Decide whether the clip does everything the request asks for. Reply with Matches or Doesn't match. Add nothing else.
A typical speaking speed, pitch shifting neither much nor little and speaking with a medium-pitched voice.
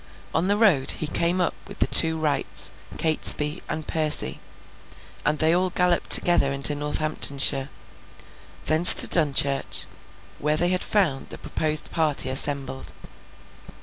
Doesn't match